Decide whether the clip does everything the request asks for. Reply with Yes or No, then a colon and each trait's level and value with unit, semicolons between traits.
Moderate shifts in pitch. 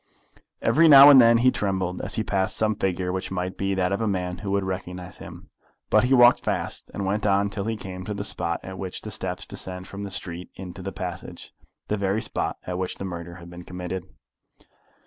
No: narrow, 2.3 semitones